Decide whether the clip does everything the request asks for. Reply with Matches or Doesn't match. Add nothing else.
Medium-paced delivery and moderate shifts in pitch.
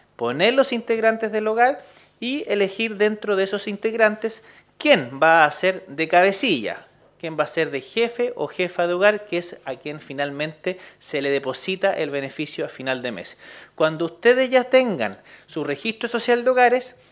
Doesn't match